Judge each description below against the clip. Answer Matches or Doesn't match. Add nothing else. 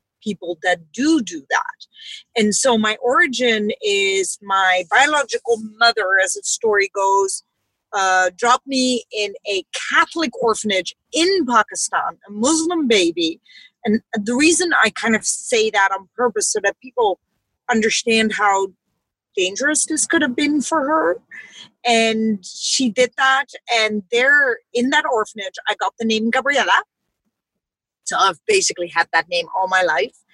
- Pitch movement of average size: Doesn't match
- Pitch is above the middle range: Matches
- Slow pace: Doesn't match